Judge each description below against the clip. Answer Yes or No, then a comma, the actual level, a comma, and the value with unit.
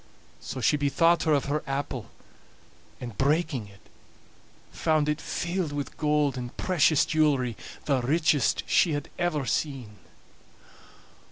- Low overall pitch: No, medium, 145 Hz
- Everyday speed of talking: No, slow, 125 wpm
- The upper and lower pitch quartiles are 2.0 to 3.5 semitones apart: Yes, average, 2.9 semitones